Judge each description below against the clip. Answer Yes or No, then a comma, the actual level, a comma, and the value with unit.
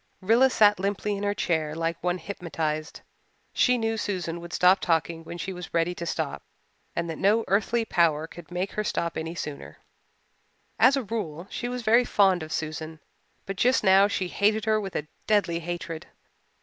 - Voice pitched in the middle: Yes, medium, 180 Hz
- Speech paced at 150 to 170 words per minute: No, average, 185 wpm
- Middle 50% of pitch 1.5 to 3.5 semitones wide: No, average, 4.1 semitones